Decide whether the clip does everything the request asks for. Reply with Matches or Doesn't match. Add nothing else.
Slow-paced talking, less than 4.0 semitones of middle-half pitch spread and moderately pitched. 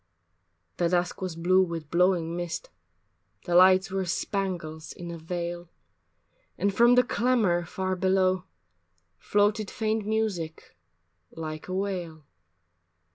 Matches